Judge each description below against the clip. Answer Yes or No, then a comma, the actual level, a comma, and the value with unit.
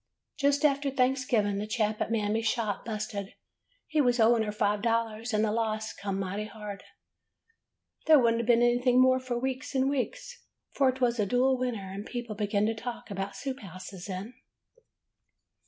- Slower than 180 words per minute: No, average, 185 wpm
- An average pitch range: Yes, average, 3.4 semitones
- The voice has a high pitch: Yes, high, 230 Hz